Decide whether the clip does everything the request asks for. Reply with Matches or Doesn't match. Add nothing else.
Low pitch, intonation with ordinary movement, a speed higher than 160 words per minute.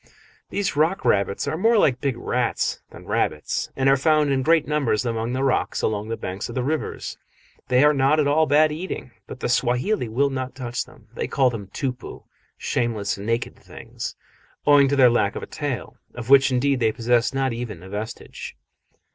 Matches